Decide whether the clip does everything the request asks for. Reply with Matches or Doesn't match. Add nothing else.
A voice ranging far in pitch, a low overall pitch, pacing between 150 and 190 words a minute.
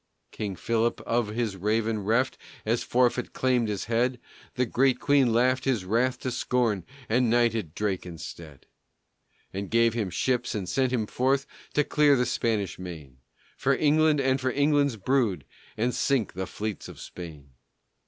Doesn't match